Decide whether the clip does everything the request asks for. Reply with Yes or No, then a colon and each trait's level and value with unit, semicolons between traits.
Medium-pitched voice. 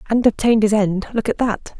No: high, 215 Hz